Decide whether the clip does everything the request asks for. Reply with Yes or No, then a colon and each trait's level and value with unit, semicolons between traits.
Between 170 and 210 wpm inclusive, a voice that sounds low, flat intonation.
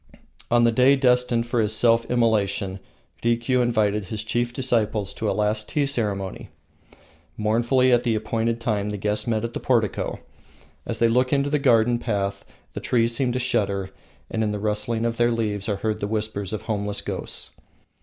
Yes: average, 185 wpm; low, 115 Hz; narrow, 2.3 semitones